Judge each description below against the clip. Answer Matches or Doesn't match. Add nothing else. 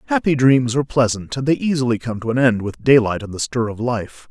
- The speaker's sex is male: Matches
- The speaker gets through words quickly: Matches